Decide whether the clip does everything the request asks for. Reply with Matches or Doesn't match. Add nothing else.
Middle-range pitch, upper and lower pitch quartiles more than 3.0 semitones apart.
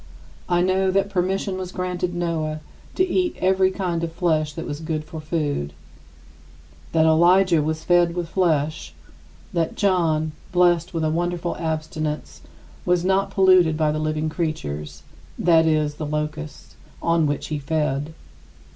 Doesn't match